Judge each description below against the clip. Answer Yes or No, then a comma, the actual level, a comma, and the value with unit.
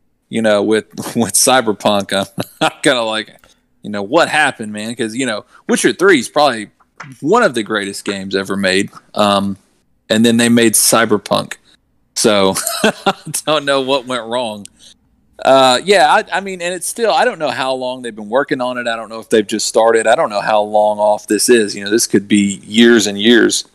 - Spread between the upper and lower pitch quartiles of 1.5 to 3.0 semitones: No, average, 3.9 semitones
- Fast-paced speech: Yes, fast, 210 wpm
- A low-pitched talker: Yes, low, 110 Hz